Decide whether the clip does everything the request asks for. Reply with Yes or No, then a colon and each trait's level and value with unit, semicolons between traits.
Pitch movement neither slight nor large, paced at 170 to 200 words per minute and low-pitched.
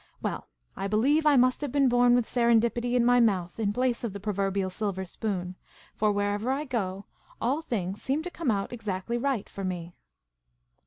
No: average, 4.0 semitones; average, 190 wpm; high, 225 Hz